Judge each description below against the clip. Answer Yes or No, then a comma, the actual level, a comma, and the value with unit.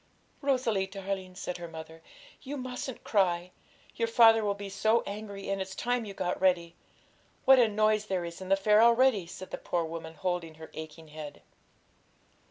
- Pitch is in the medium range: No, high, 195 Hz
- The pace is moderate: Yes, average, 180 wpm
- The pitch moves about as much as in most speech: Yes, average, 4.1 semitones